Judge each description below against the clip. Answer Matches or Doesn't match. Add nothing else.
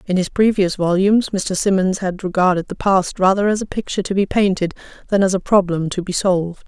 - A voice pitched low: Doesn't match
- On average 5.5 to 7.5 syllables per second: Matches